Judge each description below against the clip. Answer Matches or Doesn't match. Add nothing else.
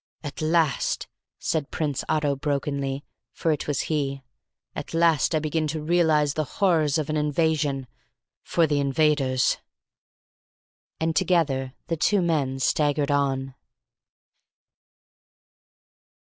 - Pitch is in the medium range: Matches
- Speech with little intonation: Matches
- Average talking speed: Doesn't match